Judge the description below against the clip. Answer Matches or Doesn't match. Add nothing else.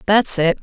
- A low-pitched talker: Doesn't match